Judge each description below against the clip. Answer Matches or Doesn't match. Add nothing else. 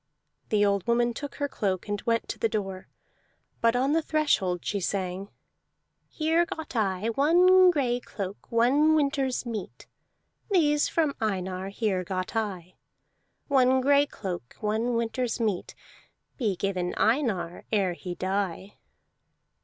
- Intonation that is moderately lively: Doesn't match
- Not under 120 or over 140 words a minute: Matches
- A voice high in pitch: Matches